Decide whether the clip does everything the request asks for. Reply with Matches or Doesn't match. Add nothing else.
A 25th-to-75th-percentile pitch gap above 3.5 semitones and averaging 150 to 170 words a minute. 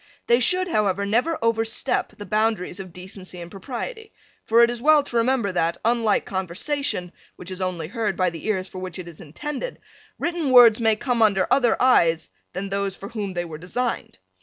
Doesn't match